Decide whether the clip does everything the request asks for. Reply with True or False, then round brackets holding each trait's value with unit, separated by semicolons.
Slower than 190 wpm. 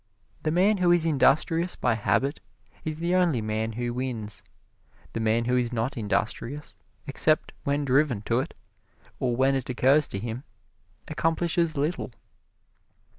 True (145 wpm)